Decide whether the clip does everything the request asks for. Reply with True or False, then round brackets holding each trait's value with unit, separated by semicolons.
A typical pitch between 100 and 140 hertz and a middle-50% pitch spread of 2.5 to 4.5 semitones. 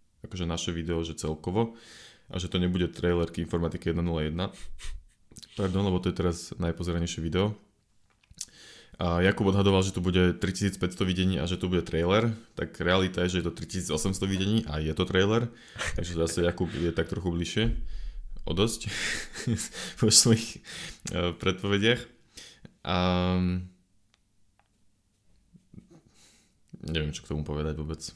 False (90 Hz; 2.9 semitones)